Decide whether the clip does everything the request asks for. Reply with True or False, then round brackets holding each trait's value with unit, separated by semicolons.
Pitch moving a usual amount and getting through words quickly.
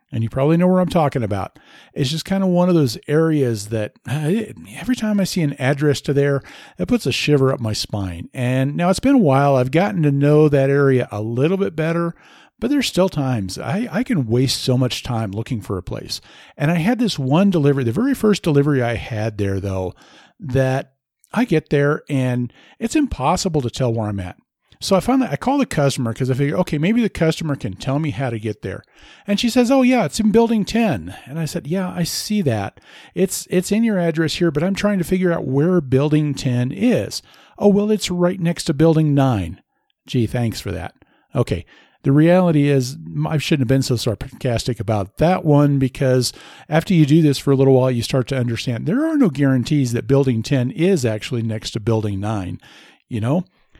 False (6.2 semitones; 215 wpm)